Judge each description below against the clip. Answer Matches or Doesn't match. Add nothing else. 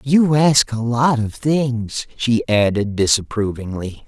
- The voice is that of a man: Matches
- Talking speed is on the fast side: Doesn't match